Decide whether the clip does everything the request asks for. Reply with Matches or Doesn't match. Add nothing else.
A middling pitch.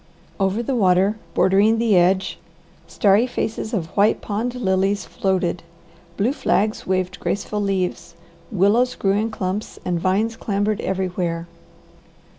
Doesn't match